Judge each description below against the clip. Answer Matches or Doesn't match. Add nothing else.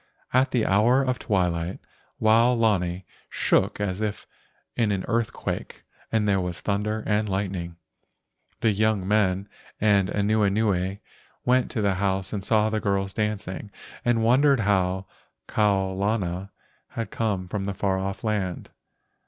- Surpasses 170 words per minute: Doesn't match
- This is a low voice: Matches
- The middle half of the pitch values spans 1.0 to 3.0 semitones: Matches